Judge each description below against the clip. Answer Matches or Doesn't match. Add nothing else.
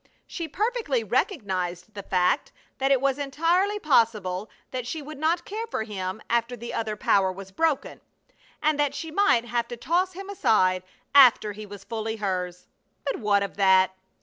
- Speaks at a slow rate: Doesn't match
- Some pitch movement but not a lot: Doesn't match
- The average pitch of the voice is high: Matches